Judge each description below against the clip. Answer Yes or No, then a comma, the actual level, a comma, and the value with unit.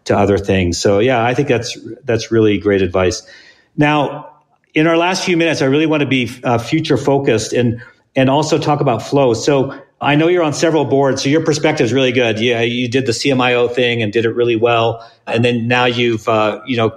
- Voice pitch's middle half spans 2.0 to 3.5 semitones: No, average, 4.1 semitones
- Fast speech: Yes, fast, 225 wpm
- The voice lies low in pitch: Yes, low, 125 Hz